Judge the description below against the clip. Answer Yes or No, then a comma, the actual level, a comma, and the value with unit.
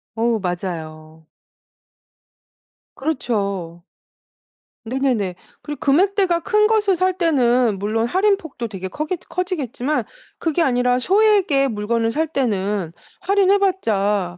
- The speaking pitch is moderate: No, very high, 255 Hz